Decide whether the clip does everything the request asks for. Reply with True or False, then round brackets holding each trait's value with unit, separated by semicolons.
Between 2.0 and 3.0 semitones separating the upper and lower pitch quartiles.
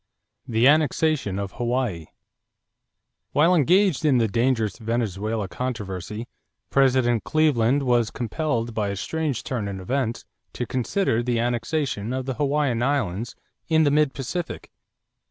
False (4.4 semitones)